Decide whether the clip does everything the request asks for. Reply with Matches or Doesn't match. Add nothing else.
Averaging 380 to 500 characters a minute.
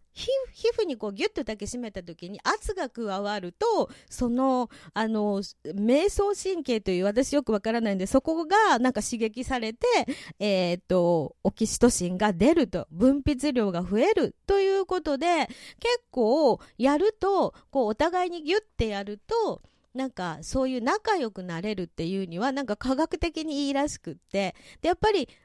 Doesn't match